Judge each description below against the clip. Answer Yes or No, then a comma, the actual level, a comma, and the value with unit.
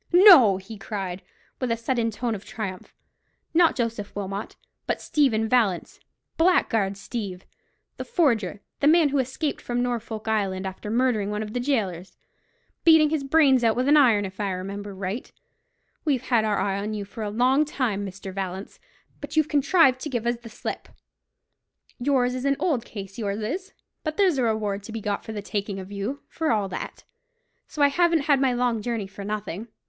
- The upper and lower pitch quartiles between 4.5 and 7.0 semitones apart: Yes, average, 5.2 semitones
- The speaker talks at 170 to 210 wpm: Yes, average, 185 wpm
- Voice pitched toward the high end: Yes, high, 225 Hz